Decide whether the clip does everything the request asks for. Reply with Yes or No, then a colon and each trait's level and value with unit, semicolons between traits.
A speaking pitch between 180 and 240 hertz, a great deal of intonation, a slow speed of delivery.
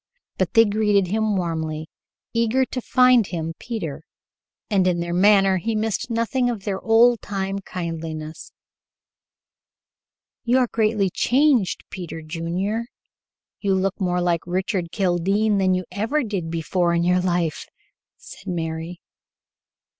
No: high, 190 Hz; average, 4.3 semitones; slow, 130 wpm